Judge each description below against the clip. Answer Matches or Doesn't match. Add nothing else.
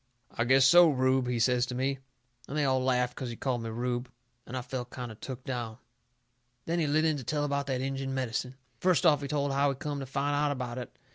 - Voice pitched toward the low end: Matches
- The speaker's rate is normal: Doesn't match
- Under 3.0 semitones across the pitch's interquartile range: Matches